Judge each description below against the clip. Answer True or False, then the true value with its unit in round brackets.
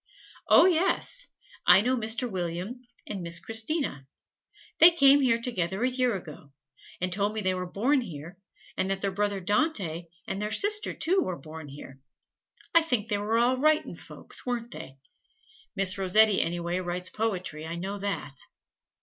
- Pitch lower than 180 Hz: False (205 Hz)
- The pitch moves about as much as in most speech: False (5.8 semitones)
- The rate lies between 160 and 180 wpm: True (165 wpm)